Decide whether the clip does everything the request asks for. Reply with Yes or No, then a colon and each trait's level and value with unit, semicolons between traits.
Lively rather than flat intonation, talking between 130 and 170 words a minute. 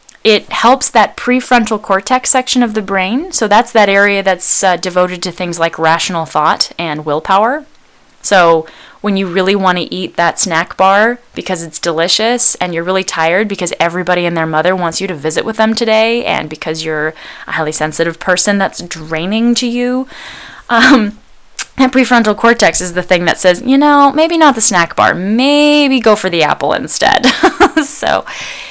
No: wide, 5.8 semitones; average, 180 wpm